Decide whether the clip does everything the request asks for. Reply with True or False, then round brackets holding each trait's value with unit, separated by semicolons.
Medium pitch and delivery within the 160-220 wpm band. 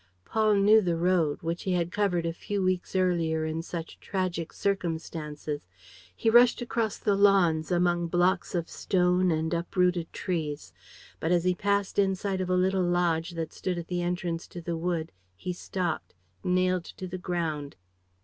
True (175 Hz; 170 wpm)